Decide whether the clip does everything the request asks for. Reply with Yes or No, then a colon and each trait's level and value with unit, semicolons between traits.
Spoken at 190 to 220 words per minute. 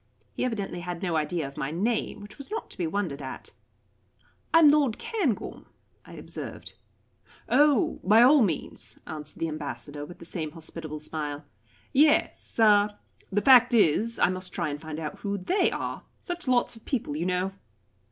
No: average, 175 wpm